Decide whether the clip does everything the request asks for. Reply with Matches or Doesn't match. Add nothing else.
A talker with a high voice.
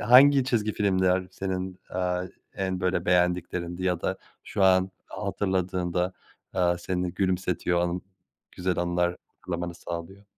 Doesn't match